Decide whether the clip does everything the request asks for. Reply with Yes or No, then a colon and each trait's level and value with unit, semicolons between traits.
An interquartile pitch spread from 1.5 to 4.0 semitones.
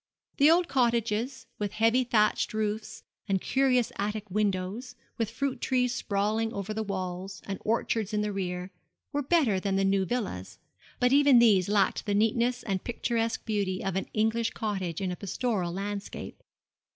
Yes: average, 3.4 semitones